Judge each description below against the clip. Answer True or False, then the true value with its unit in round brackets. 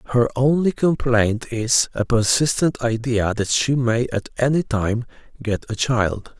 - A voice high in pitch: False (120 Hz)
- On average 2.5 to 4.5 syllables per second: True (4.1 syllables/s)